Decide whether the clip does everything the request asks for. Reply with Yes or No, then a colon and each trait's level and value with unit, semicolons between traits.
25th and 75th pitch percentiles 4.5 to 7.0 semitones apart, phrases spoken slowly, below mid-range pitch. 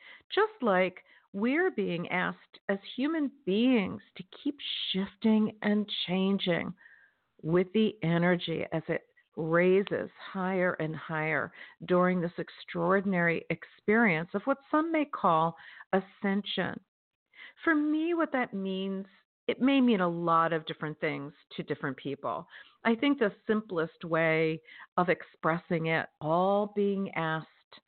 No: average, 4.9 semitones; slow, 125 wpm; high, 190 Hz